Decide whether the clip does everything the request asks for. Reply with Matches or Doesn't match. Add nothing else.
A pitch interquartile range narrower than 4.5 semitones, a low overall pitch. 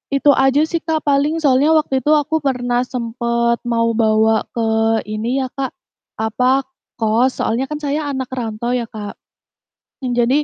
Doesn't match